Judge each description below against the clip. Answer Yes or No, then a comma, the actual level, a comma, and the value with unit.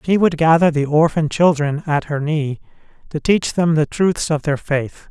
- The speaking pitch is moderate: Yes, medium, 155 Hz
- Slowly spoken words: No, average, 200 wpm